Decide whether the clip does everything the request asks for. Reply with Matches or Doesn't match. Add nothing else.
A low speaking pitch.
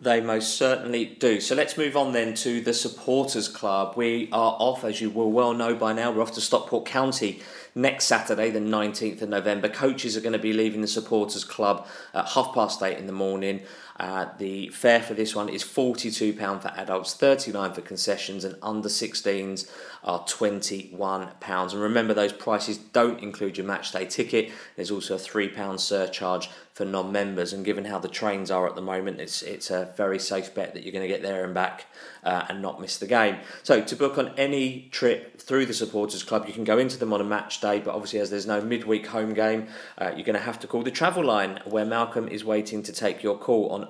Matches